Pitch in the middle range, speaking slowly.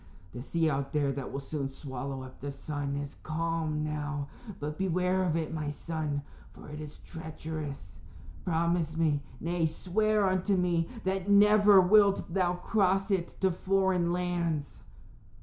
No: medium, 165 Hz; average, 150 wpm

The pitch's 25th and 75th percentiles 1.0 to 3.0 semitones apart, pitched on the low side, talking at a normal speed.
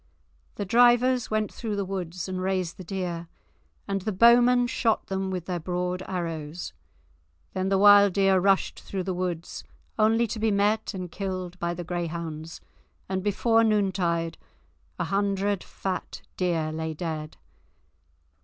No: average, 2.7 semitones; high, 190 Hz; average, 145 wpm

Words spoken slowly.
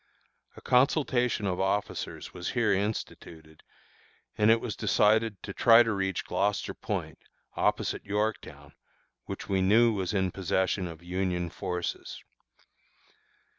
Yes: slow, 125 wpm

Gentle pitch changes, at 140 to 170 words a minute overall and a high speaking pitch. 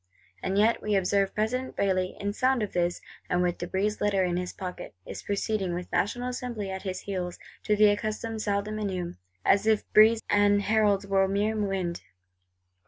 No: narrow, 2.2 semitones; average, 190 wpm; high, 200 Hz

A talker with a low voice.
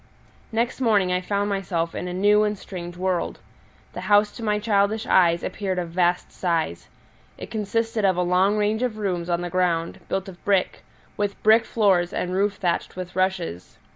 No: high, 190 Hz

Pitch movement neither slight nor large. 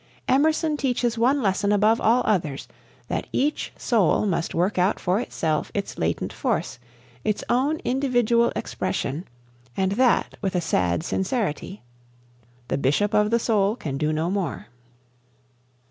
No: wide, 6.1 semitones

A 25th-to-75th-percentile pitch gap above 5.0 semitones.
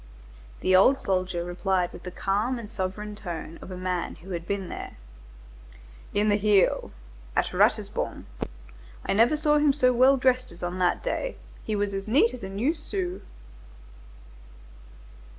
Yes: wide, 5.6 semitones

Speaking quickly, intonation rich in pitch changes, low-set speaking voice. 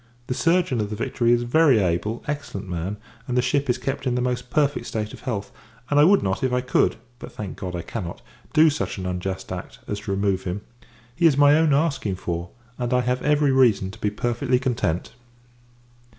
Yes: fast, 220 wpm; wide, 5.9 semitones; low, 120 Hz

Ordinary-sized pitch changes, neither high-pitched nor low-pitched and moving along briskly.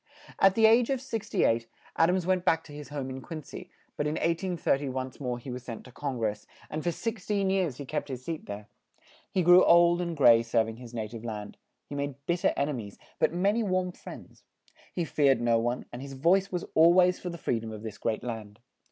No: wide, 6.9 semitones; medium, 145 Hz; fast, 250 wpm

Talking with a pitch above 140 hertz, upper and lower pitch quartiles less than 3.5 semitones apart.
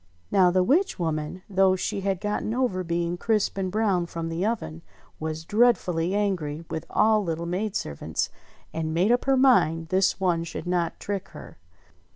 No: medium, 185 Hz; average, 3.9 semitones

